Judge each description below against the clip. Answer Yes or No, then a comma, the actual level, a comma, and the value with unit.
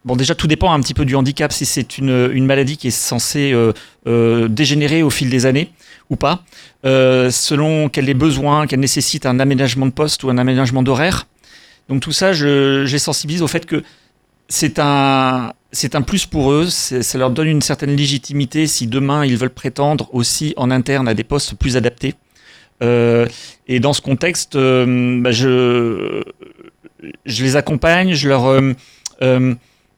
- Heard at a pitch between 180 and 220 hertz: No, low, 135 Hz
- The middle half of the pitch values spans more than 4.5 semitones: No, average, 2.7 semitones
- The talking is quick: No, average, 185 wpm